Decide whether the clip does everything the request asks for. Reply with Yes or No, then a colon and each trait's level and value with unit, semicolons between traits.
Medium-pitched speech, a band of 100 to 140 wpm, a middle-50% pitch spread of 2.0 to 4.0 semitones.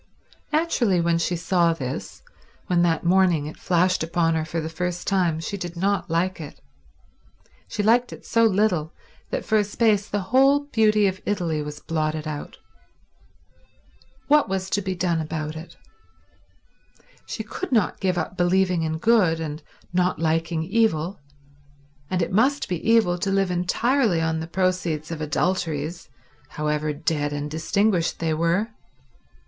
No: medium, 175 Hz; average, 155 wpm; average, 3.7 semitones